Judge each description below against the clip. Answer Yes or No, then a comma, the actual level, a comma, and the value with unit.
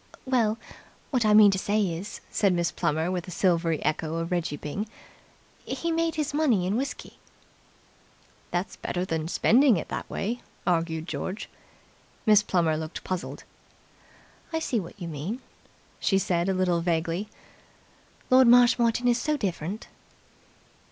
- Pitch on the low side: No, high, 190 Hz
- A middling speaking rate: Yes, average, 145 wpm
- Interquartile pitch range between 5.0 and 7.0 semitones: Yes, wide, 5.6 semitones